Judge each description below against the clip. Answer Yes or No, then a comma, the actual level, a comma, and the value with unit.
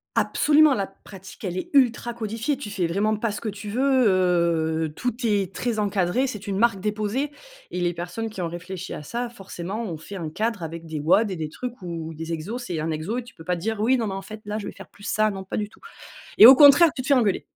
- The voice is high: Yes, high, 205 Hz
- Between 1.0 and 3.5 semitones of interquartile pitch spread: No, average, 4.9 semitones